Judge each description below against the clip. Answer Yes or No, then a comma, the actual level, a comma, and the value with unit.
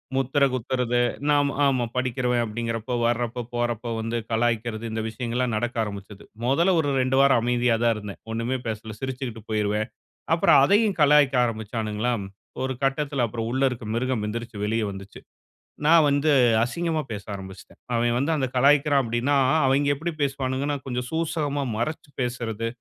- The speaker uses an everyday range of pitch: Yes, average, 3.3 semitones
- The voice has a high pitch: No, low, 125 Hz